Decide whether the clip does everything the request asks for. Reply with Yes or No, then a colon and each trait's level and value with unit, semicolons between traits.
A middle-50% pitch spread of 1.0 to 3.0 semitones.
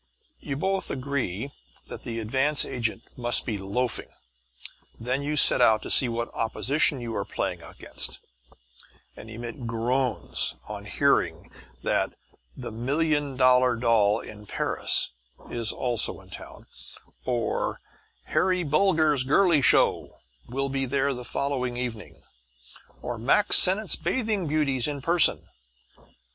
No: average, 3.9 semitones